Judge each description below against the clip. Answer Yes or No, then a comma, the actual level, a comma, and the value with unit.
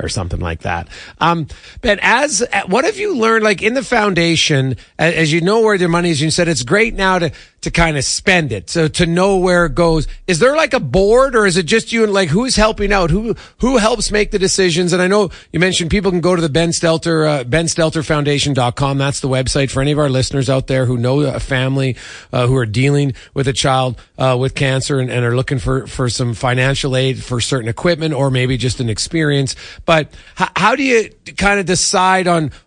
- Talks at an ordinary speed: No, fast, 230 wpm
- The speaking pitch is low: No, medium, 160 Hz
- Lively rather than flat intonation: Yes, wide, 6.2 semitones